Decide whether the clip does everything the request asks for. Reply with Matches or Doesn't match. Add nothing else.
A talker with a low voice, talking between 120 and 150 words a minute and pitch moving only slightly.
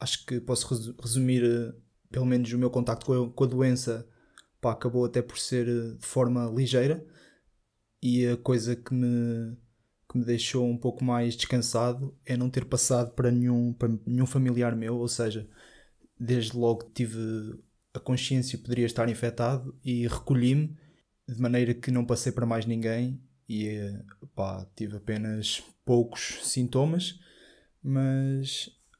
Matches